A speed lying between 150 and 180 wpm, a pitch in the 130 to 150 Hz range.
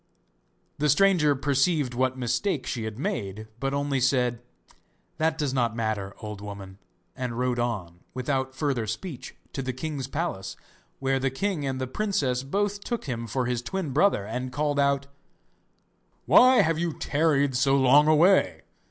Yes: average, 160 wpm; low, 135 Hz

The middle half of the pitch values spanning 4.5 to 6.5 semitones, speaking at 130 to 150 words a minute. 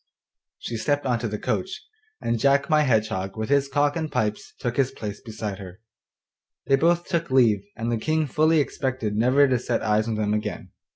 No: average, 5.0 semitones; average, 190 wpm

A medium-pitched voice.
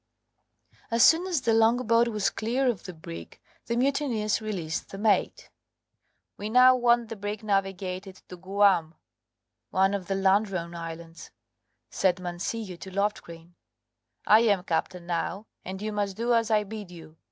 No: high, 200 Hz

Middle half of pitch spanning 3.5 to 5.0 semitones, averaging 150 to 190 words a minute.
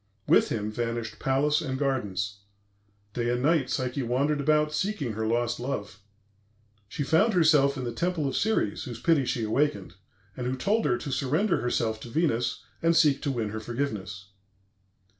Yes: average, 4.5 semitones; average, 170 wpm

